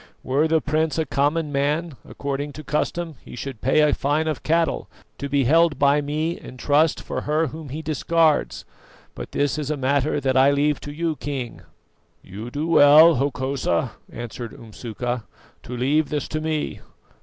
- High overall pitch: No, medium, 145 Hz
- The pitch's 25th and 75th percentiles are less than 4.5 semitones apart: Yes, narrow, 2.5 semitones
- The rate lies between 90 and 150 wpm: No, average, 175 wpm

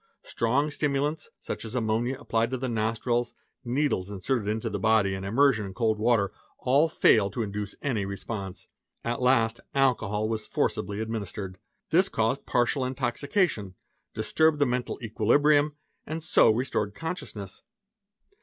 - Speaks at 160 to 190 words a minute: No, average, 145 wpm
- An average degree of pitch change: Yes, average, 4.4 semitones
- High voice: No, low, 115 Hz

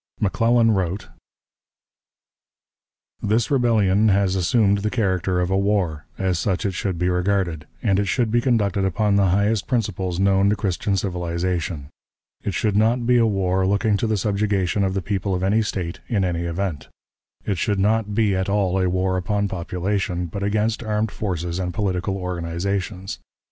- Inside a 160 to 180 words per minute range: Yes, average, 170 wpm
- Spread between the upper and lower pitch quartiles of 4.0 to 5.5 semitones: No, narrow, 2.5 semitones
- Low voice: Yes, low, 100 Hz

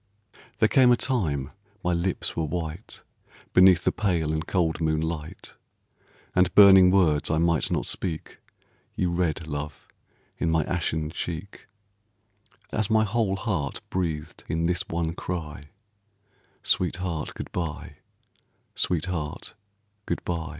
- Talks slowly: Yes, slow, 125 wpm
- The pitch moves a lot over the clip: No, average, 2.7 semitones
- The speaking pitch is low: Yes, very low, 85 Hz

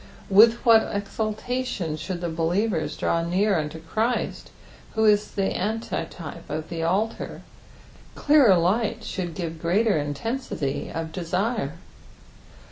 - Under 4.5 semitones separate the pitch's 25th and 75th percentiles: No, average, 5.0 semitones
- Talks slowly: Yes, slow, 120 wpm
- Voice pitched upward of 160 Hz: Yes, high, 190 Hz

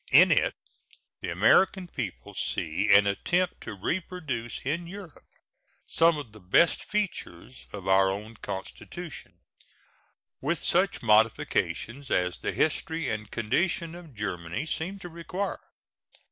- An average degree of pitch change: No, wide, 8.9 semitones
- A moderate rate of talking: No, slow, 125 wpm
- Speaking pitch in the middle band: No, low, 130 Hz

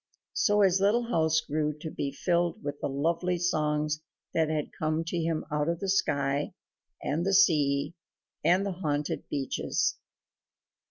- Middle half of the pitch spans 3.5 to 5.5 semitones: No, average, 3.1 semitones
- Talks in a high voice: No, medium, 160 Hz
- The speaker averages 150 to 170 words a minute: Yes, average, 155 wpm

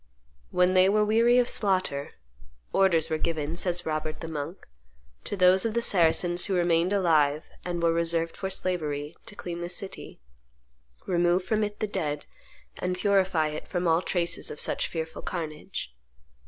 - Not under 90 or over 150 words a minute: No, average, 165 wpm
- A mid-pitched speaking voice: Yes, medium, 175 Hz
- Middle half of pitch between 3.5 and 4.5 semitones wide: No, average, 2.9 semitones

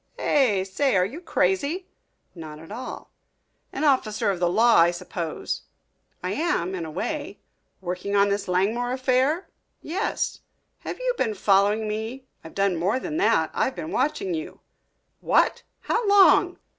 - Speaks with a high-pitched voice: Yes, high, 230 Hz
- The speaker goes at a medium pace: Yes, average, 155 wpm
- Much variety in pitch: Yes, wide, 8.3 semitones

